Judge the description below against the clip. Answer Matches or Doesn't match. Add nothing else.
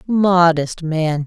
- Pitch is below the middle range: Doesn't match